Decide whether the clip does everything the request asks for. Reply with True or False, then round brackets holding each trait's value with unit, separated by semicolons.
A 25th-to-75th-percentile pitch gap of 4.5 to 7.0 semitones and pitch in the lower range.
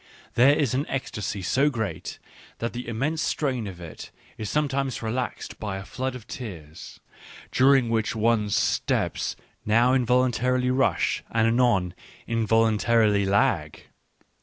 False (3.4 semitones; 115 Hz)